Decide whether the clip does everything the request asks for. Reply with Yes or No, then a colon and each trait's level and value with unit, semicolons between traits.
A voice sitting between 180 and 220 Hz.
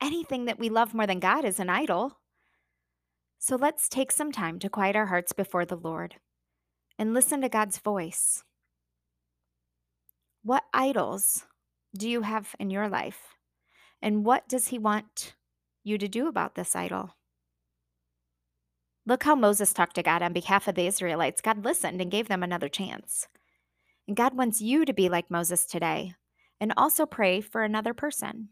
Yes: high, 190 Hz